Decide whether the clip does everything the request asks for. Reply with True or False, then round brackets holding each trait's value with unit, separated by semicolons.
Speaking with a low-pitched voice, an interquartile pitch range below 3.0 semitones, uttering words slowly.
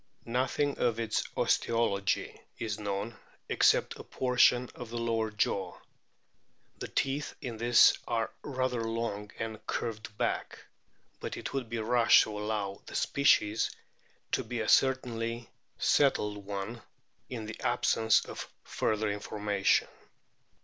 True (115 Hz; 2.5 semitones; 130 wpm)